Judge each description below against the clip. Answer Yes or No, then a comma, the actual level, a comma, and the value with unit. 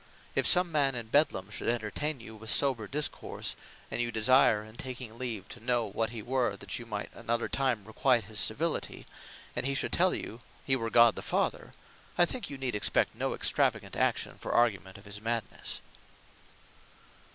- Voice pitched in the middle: No, low, 120 Hz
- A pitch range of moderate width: Yes, average, 3.4 semitones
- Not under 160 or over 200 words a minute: Yes, average, 185 wpm